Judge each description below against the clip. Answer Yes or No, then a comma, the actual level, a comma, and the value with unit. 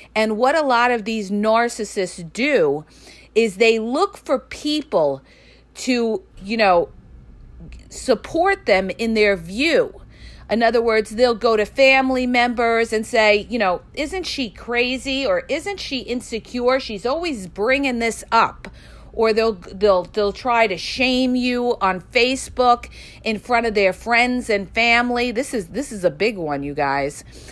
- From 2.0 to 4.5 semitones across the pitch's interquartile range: Yes, average, 3.6 semitones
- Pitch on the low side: No, high, 230 Hz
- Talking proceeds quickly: No, average, 155 wpm